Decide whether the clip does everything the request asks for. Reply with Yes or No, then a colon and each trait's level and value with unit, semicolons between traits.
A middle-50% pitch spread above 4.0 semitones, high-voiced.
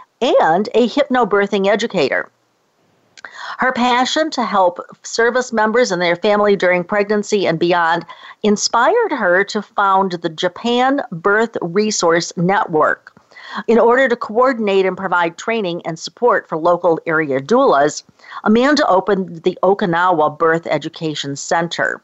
Yes: average, 4.9 semitones; high, 200 Hz